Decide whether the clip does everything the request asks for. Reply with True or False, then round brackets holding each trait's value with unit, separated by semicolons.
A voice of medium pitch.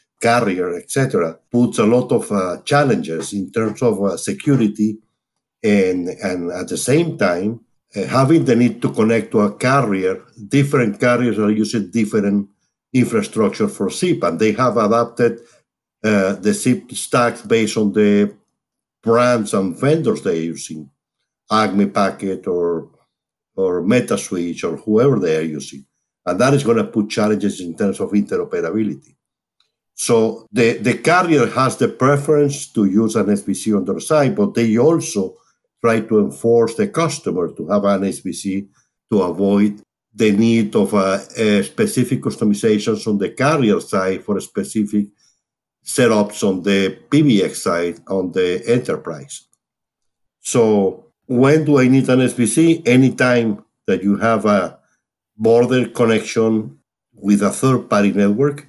False (110 Hz)